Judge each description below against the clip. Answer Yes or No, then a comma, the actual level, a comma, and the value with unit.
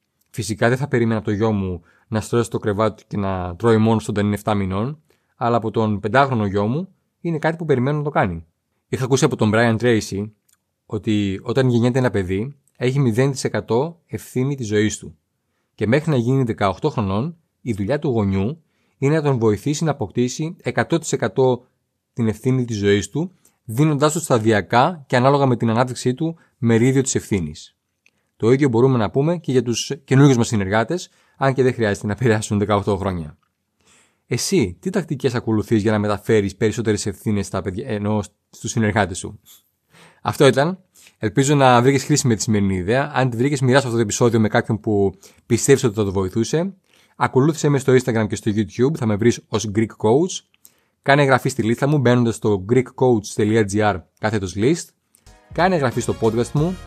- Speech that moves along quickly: Yes, fast, 180 wpm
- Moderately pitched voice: No, low, 115 Hz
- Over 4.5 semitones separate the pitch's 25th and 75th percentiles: No, average, 4.2 semitones